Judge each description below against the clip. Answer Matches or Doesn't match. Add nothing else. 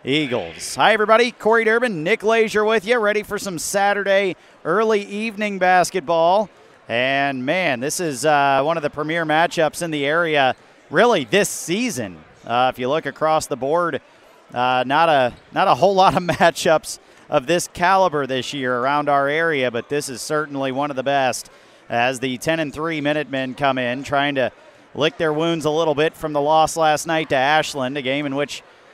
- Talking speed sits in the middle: Matches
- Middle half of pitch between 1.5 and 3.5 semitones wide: Doesn't match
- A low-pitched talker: Doesn't match